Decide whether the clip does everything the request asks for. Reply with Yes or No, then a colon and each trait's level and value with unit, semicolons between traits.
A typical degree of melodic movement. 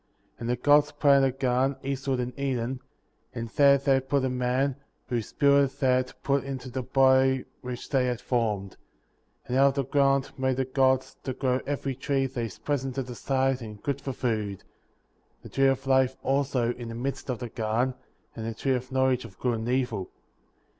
No: narrow, 1.7 semitones